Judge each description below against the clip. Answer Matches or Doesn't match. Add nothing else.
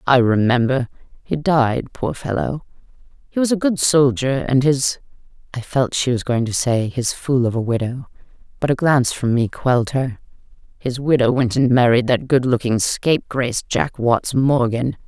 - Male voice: Doesn't match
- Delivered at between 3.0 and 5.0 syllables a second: Matches